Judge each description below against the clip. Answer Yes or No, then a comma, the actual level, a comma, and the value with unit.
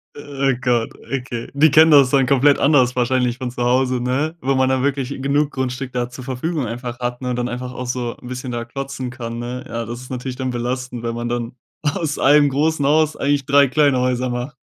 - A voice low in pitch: Yes, low, 130 Hz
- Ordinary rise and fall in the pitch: No, narrow, 2.2 semitones